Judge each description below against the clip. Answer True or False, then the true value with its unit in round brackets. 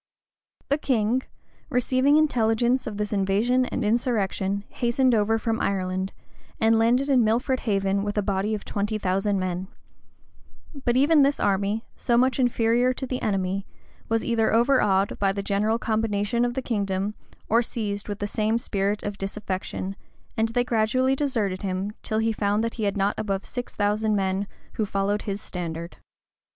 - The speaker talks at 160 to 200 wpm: True (165 wpm)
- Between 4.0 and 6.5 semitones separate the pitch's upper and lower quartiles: False (3.2 semitones)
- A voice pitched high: True (215 Hz)